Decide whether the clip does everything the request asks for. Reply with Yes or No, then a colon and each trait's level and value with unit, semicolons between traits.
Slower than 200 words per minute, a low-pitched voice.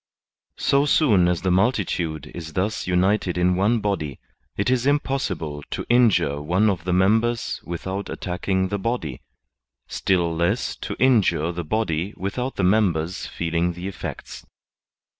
Yes: average, 140 wpm; very low, 95 Hz